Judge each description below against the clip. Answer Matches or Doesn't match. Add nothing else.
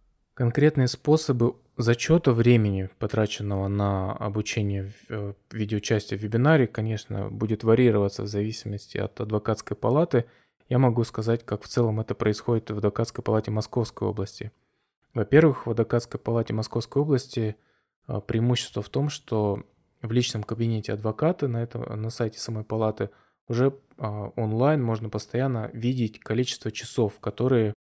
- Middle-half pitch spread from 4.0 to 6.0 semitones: Doesn't match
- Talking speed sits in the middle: Matches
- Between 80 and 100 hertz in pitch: Doesn't match